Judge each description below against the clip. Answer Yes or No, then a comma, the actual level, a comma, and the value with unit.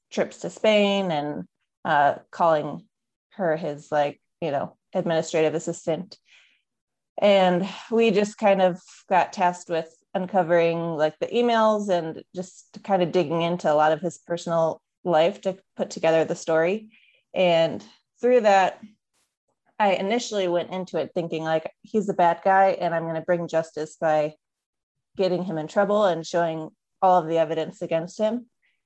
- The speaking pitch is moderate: Yes, medium, 180 Hz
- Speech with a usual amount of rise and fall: Yes, average, 3.5 semitones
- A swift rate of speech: No, average, 155 wpm